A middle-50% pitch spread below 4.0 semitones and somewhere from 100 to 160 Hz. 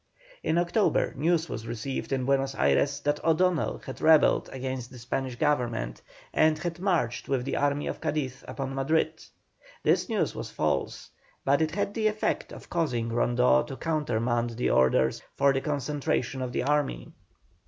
No: average, 4.4 semitones; low, 135 Hz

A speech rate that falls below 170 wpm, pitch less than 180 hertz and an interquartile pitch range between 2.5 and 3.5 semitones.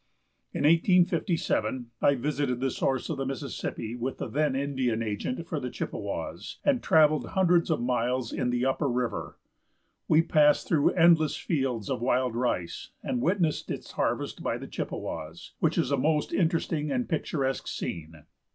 No: average, 160 wpm; low, 135 Hz; average, 4.5 semitones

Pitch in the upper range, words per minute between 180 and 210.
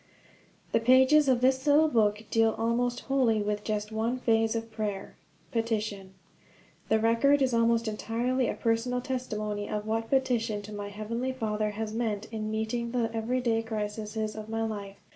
No: high, 225 Hz; average, 165 wpm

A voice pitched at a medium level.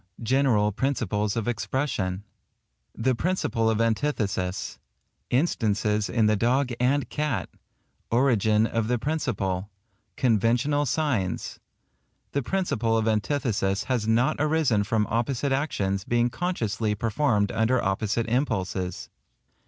No: low, 115 Hz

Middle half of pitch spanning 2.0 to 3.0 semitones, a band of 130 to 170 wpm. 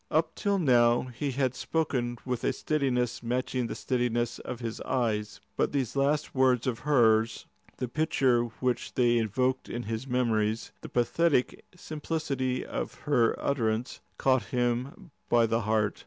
Yes: average, 2.7 semitones; average, 150 wpm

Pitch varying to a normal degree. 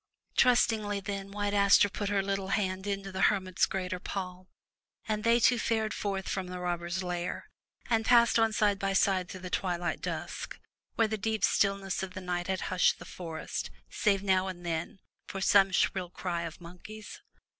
No: narrow, 2.1 semitones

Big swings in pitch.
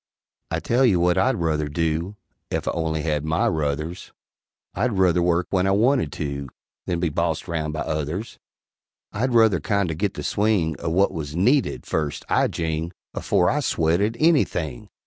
No: average, 4.3 semitones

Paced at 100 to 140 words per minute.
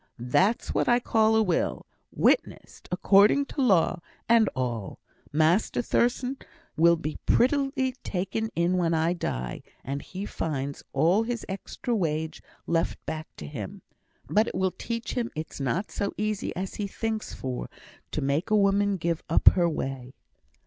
No: average, 155 wpm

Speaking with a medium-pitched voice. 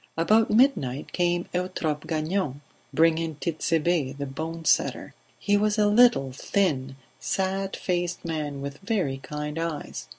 Yes: medium, 165 Hz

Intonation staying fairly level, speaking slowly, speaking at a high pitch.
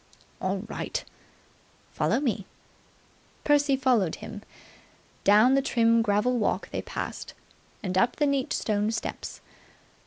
No: average, 4.5 semitones; slow, 120 wpm; high, 230 Hz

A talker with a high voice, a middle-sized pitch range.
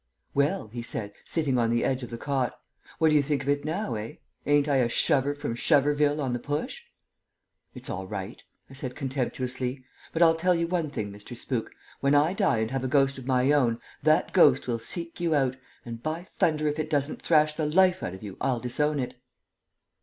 No: medium, 140 Hz; average, 3.8 semitones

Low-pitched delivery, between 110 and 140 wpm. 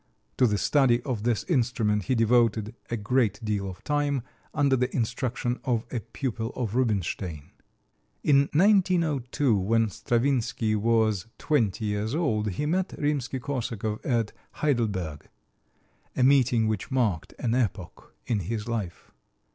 Yes: low, 115 Hz; slow, 135 wpm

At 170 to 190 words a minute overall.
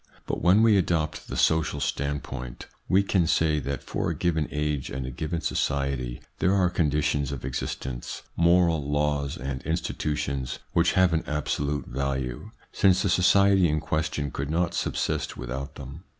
No: average, 160 wpm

